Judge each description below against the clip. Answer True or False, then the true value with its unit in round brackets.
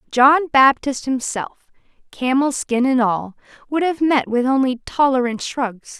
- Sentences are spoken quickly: False (140 wpm)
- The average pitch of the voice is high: True (260 Hz)